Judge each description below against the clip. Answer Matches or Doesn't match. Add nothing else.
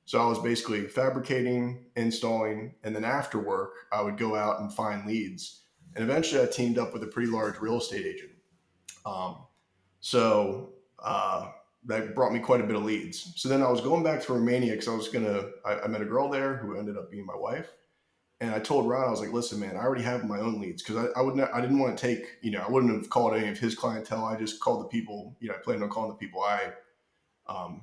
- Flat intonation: Doesn't match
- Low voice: Matches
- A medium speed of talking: Doesn't match